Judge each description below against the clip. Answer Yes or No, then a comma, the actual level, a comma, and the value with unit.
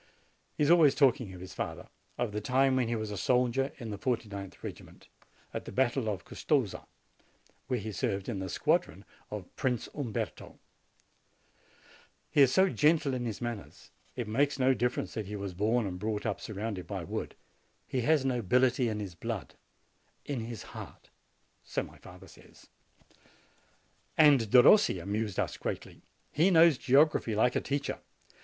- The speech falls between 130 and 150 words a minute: No, average, 170 wpm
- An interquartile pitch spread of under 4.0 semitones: No, average, 4.3 semitones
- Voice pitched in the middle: No, low, 120 Hz